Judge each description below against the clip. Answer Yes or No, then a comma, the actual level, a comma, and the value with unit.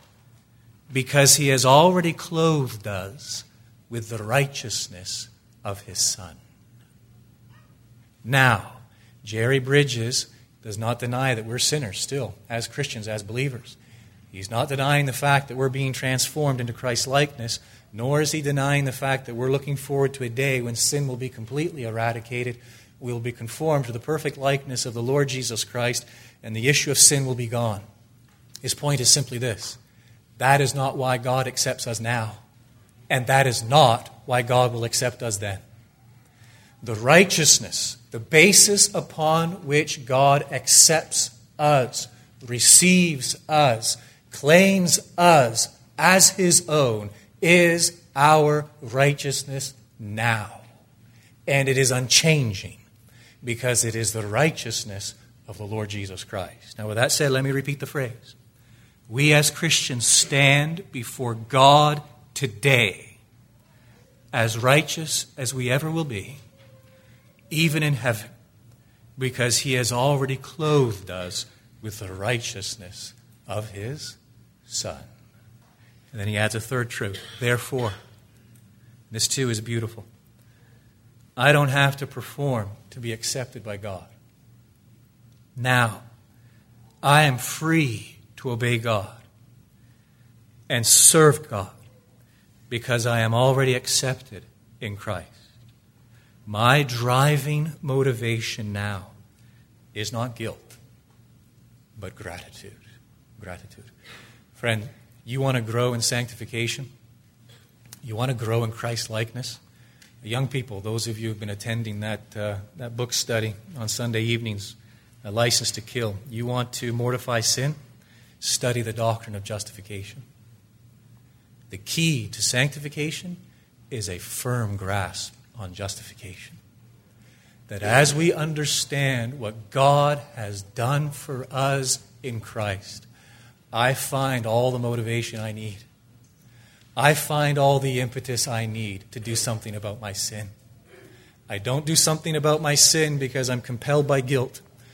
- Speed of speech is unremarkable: No, slow, 130 wpm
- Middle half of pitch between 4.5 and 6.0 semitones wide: No, average, 2.9 semitones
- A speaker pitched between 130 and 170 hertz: No, low, 120 Hz